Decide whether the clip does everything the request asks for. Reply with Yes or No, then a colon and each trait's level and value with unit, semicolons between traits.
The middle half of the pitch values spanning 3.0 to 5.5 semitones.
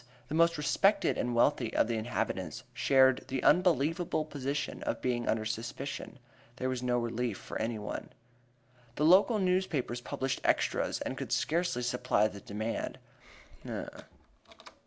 Yes: average, 5.0 semitones